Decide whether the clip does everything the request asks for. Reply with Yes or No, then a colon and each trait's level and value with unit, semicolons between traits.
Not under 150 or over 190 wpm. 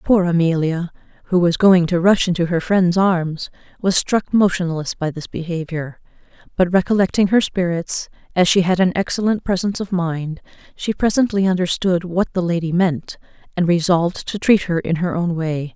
Yes: average, 175 wpm